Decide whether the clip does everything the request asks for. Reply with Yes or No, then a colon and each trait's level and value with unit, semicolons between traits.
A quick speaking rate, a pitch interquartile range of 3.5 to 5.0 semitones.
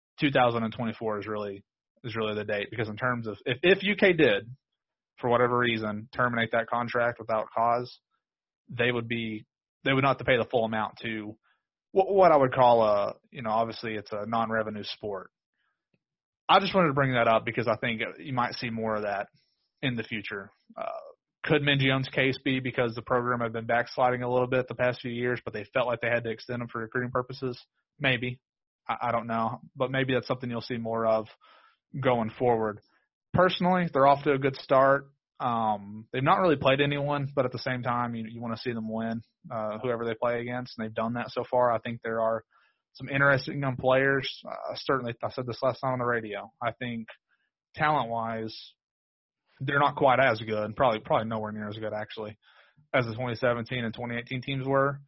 No: fast, 210 wpm; average, 2.7 semitones